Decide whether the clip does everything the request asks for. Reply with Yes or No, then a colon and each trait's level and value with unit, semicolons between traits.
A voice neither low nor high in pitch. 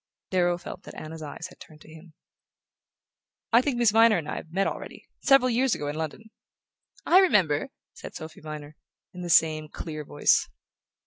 Yes: medium, 170 Hz